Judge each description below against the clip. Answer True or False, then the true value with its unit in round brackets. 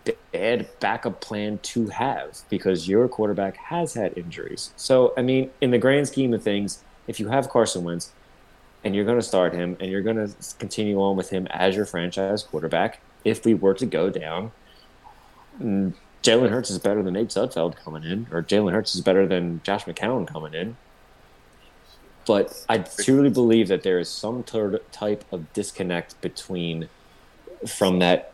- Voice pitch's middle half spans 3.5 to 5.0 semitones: True (3.9 semitones)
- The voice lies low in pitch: True (105 Hz)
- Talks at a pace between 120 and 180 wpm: True (175 wpm)